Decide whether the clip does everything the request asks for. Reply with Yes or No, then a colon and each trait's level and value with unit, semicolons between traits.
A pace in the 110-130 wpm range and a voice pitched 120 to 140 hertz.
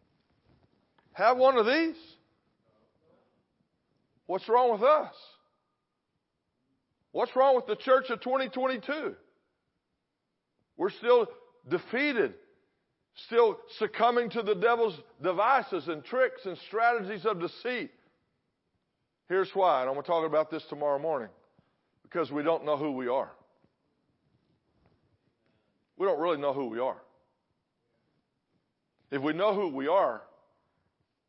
No: slow, 115 wpm; high, 235 Hz